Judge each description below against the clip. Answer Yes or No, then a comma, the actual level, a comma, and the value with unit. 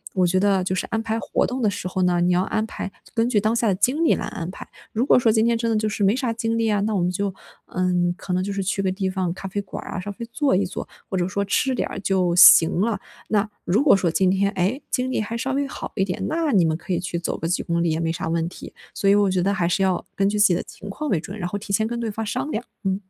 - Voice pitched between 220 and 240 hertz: No, high, 200 Hz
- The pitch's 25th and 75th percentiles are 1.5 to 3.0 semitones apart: No, average, 3.6 semitones